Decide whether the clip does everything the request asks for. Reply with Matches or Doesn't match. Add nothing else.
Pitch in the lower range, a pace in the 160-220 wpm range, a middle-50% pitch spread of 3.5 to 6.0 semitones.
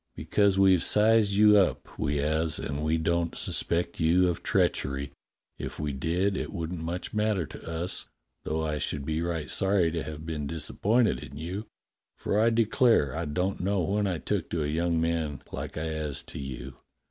Matches